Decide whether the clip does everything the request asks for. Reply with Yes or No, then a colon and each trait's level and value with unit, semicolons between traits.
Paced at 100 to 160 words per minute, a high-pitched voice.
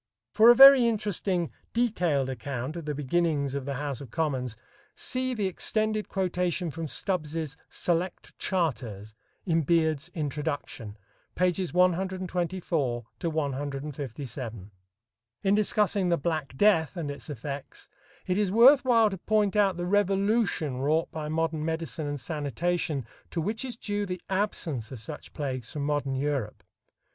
No: average, 140 wpm; medium, 165 Hz